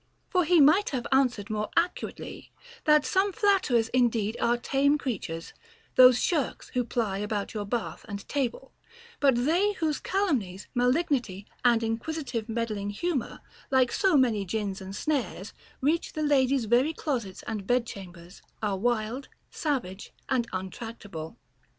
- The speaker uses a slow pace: No, average, 145 wpm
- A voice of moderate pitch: No, high, 245 Hz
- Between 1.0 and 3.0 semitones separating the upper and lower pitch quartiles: No, wide, 5.6 semitones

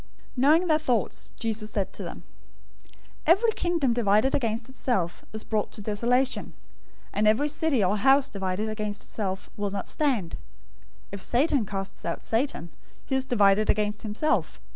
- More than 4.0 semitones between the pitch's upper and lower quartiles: Yes, average, 4.7 semitones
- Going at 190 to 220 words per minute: No, average, 160 wpm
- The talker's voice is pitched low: No, high, 220 Hz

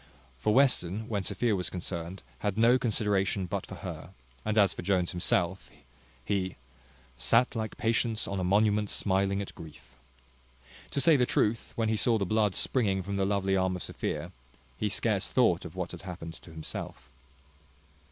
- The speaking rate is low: No, average, 170 wpm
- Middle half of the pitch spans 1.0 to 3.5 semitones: Yes, average, 2.9 semitones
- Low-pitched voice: Yes, low, 100 Hz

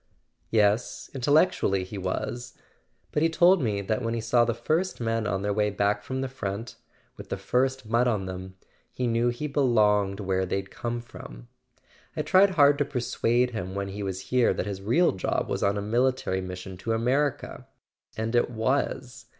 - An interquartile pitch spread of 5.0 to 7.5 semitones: No, average, 4.3 semitones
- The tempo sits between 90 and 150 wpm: No, average, 180 wpm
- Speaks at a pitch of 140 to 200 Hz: No, low, 115 Hz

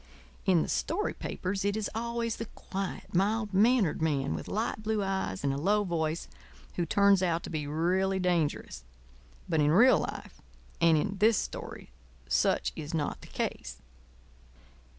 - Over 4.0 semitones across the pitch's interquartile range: Yes, average, 4.7 semitones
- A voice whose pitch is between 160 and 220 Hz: Yes, high, 190 Hz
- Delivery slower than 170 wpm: Yes, average, 160 wpm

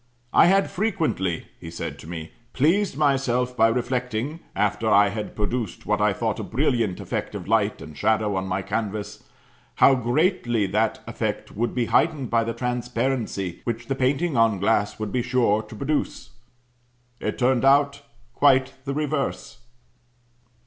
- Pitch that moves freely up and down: No, average, 4.4 semitones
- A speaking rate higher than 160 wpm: No, average, 155 wpm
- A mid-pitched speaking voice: No, low, 120 Hz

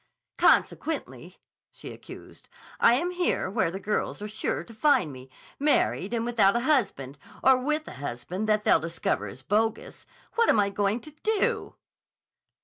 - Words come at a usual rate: Yes, average, 160 wpm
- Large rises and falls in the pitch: Yes, wide, 7.4 semitones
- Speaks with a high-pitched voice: Yes, high, 215 Hz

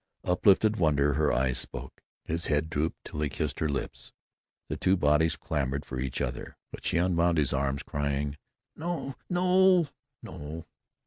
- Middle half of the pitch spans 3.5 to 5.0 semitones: Yes, average, 4.0 semitones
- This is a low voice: Yes, very low, 75 Hz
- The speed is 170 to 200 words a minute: No, average, 155 wpm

